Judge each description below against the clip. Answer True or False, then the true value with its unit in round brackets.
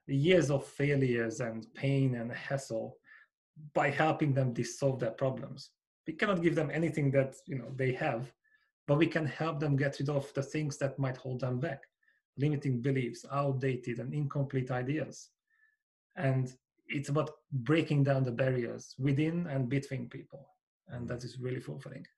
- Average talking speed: True (160 wpm)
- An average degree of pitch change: True (3.0 semitones)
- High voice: False (140 Hz)